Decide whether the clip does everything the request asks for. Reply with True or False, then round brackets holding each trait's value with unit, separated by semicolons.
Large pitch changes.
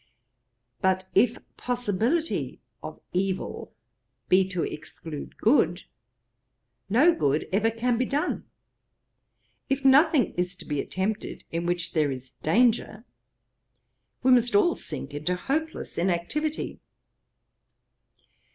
True (6.8 semitones)